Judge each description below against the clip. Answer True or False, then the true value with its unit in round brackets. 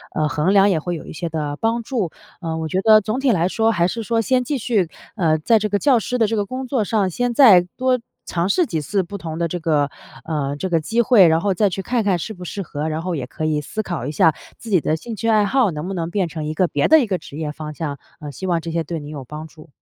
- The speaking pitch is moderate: True (180 Hz)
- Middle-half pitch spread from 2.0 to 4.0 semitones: False (5.6 semitones)